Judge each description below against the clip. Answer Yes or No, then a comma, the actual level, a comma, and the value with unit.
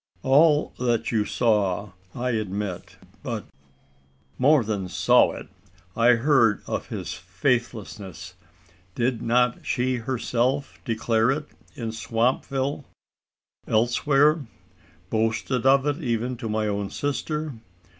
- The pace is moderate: No, slow, 115 wpm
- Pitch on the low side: Yes, low, 120 Hz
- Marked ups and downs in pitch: No, average, 3.5 semitones